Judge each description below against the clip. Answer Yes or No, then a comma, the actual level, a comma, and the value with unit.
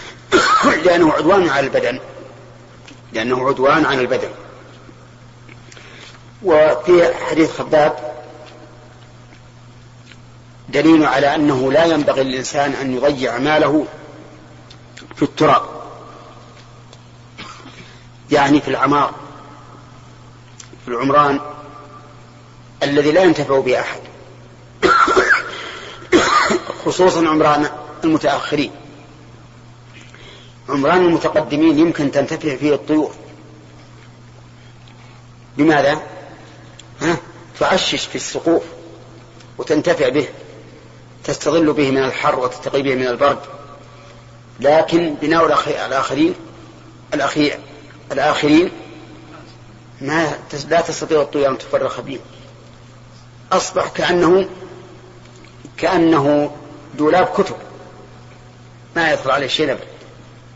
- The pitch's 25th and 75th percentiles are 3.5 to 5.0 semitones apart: Yes, average, 4.0 semitones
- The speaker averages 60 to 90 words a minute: Yes, average, 75 wpm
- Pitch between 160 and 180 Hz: No, low, 135 Hz